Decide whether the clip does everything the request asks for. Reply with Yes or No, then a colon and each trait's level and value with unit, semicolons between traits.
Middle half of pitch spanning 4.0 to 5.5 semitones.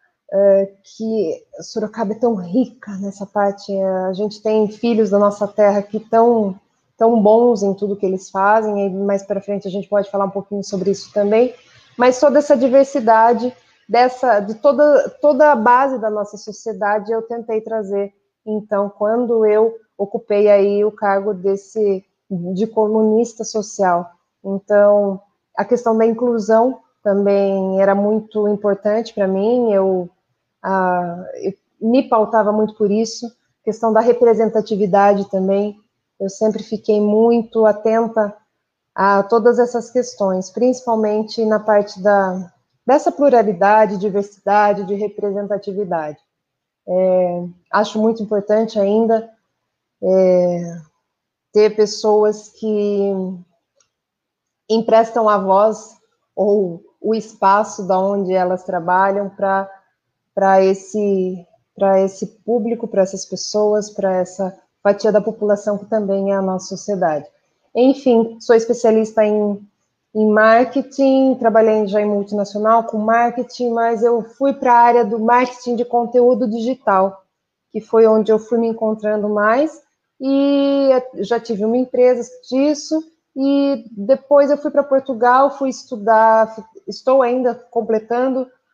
No: average, 2.7 semitones